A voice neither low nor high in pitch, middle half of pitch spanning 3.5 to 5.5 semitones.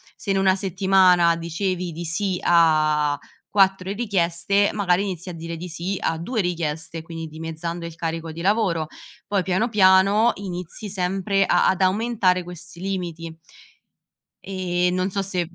No: medium, 180 Hz; average, 2.7 semitones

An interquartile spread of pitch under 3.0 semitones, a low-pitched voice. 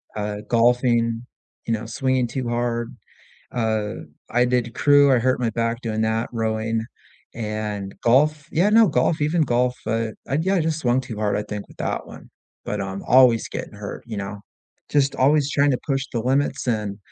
No: average, 3.4 semitones; low, 120 Hz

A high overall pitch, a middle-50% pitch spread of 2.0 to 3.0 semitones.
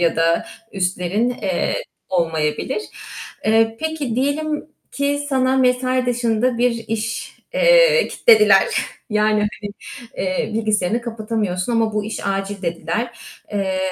No: high, 225 Hz; average, 4.6 semitones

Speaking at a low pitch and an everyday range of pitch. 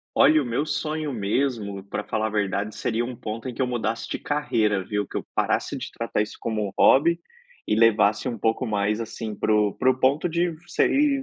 Yes: low, 115 Hz; average, 4.1 semitones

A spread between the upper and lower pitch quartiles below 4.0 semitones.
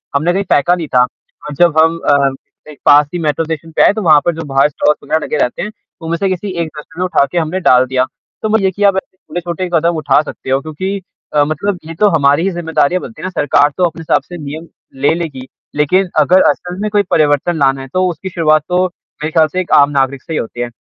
Yes: average, 3.6 semitones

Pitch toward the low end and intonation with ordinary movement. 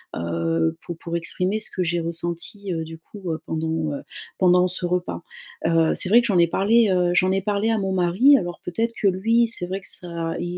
No: medium, 180 Hz; average, 3.1 semitones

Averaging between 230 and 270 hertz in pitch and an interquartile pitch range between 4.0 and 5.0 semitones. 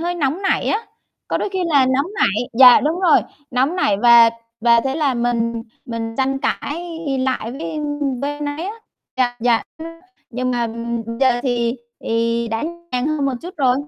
Yes: very high, 255 Hz; average, 4.5 semitones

